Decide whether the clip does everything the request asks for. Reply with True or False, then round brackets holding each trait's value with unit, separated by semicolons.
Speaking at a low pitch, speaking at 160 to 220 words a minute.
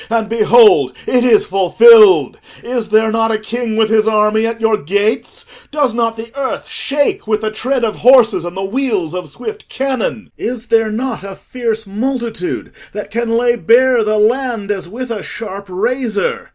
False (225 Hz; 180 wpm)